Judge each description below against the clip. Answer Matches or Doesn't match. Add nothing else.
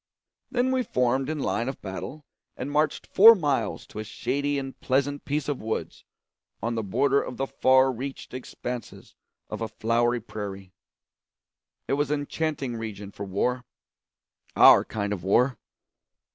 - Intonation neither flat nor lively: Matches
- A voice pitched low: Matches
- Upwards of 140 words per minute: Matches